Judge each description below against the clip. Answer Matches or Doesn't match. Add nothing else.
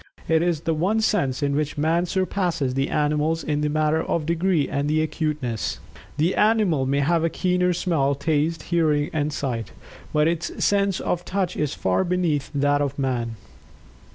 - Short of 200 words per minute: Matches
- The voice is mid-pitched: Matches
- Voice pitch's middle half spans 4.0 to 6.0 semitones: Doesn't match